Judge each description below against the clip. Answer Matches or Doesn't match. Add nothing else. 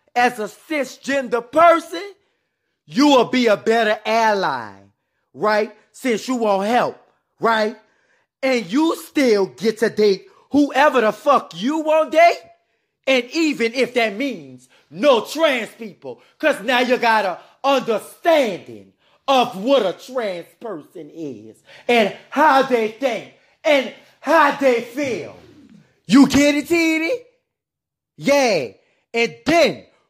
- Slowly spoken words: Matches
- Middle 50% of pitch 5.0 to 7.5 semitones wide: Matches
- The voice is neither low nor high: Doesn't match